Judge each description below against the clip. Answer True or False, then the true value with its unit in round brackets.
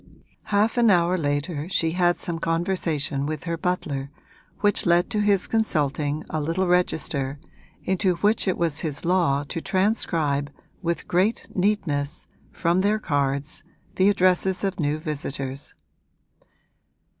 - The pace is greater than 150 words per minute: False (135 wpm)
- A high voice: False (170 Hz)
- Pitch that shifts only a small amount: False (4.4 semitones)